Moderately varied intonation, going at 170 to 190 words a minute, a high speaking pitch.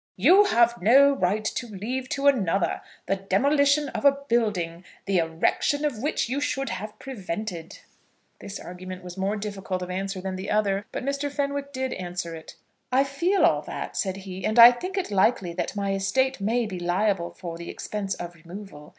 No: wide, 6.2 semitones; average, 185 wpm; high, 205 Hz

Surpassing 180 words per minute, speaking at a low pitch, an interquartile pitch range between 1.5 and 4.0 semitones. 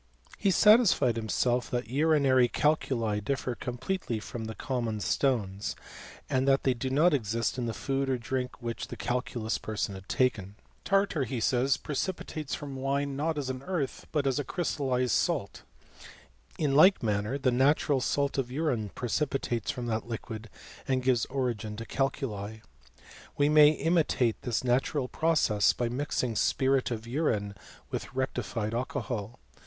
No: average, 155 wpm; low, 130 Hz; average, 3.6 semitones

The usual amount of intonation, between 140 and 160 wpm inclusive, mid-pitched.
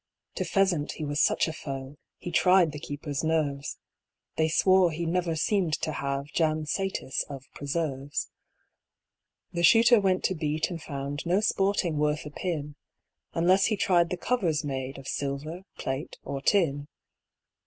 Yes: average, 4.0 semitones; average, 155 wpm; medium, 155 Hz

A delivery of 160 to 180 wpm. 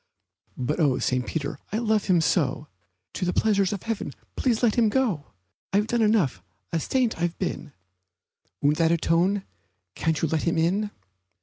Yes: average, 170 wpm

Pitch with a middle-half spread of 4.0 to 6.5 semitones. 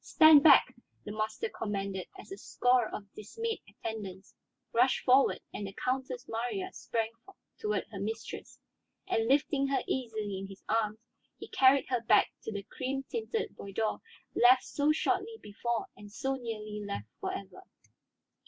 Yes: average, 4.7 semitones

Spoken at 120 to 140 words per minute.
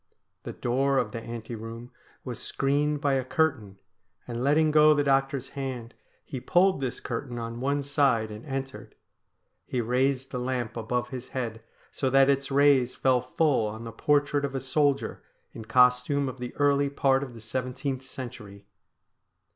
No: average, 170 wpm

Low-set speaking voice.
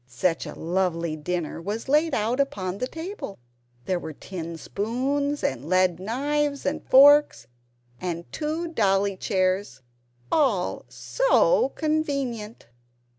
No: high, 210 Hz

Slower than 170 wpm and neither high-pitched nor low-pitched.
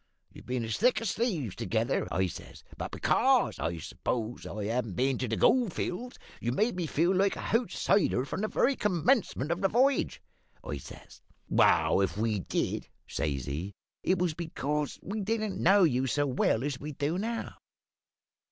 No: average, 180 wpm; medium, 150 Hz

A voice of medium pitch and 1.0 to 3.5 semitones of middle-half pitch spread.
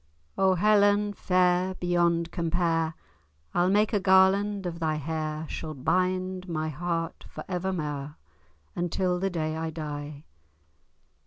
Yes: medium, 175 Hz; average, 2.9 semitones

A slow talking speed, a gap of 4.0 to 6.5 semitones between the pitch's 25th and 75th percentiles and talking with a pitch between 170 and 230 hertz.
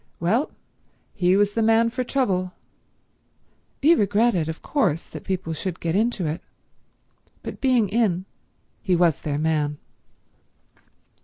Yes: slow, 130 wpm; average, 5.3 semitones; high, 190 Hz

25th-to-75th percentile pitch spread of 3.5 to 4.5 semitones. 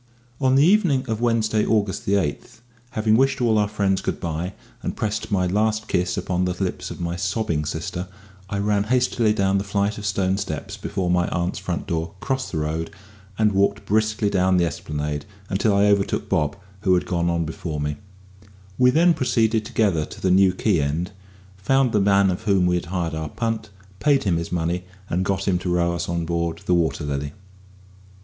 Yes: average, 3.8 semitones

